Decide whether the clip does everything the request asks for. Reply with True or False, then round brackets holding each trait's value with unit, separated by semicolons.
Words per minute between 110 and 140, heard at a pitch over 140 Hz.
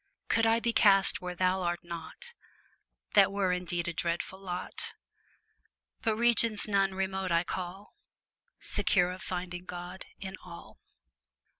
True (135 wpm; 185 Hz)